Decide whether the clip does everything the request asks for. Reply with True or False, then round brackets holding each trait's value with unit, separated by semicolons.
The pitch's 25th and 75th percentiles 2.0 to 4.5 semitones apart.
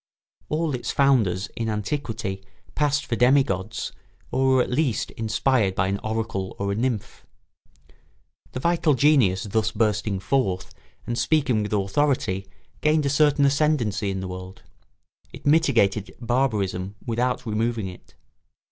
False (5.6 semitones)